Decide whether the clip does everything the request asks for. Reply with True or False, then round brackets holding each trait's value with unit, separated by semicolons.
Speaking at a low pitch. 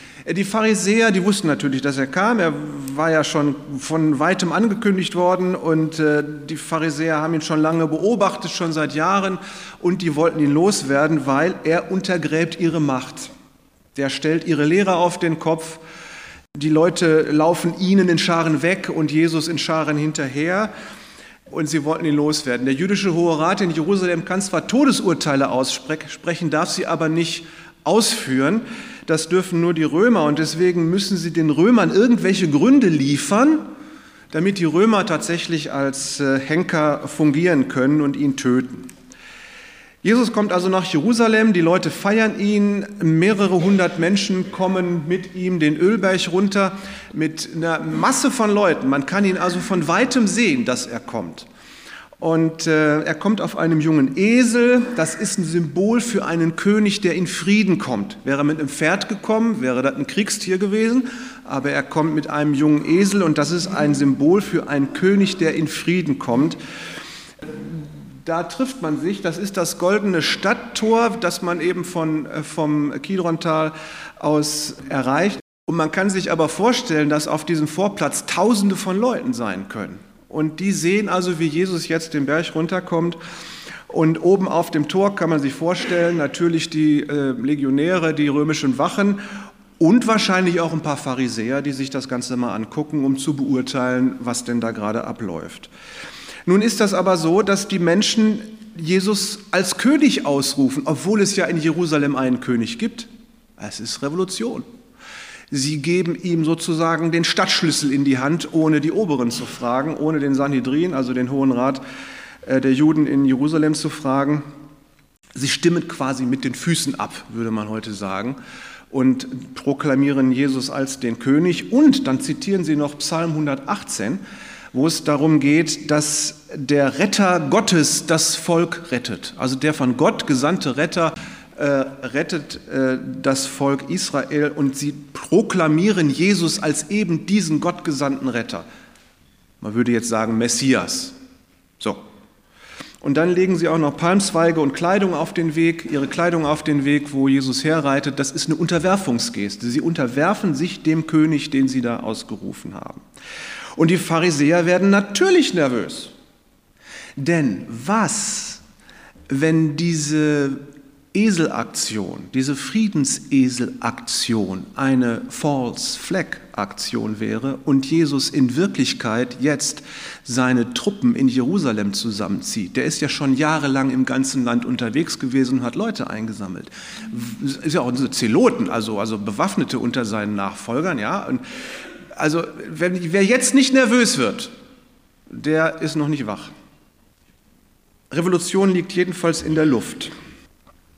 False (160 Hz)